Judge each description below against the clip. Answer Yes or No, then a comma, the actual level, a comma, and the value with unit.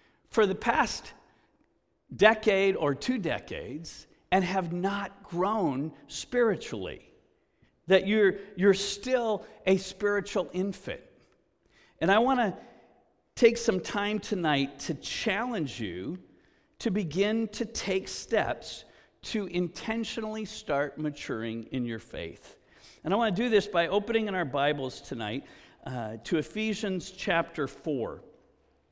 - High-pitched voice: Yes, high, 195 Hz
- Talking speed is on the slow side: Yes, slow, 120 wpm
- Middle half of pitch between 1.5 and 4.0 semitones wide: No, average, 4.7 semitones